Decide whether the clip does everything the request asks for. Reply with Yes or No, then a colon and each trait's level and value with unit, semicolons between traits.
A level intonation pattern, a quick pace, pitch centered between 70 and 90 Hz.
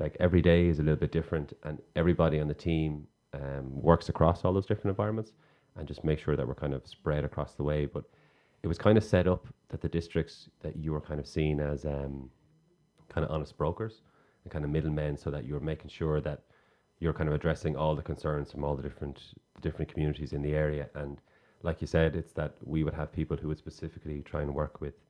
Yes: narrow, 2.1 semitones; fast, 230 wpm; very low, 75 Hz